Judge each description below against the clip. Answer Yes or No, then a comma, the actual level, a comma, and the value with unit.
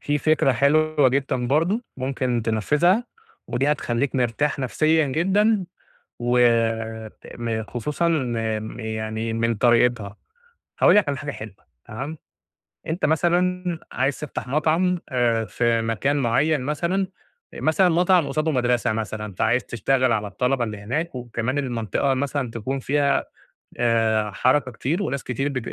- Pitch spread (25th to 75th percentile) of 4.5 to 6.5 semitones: Yes, average, 4.9 semitones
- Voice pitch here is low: Yes, low, 130 Hz